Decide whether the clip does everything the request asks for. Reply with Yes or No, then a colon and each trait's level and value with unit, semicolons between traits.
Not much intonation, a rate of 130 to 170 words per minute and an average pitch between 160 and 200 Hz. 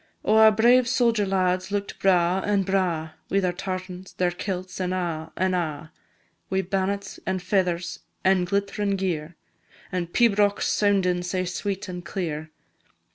Yes: narrow, 2.0 semitones; average, 145 wpm; medium, 185 Hz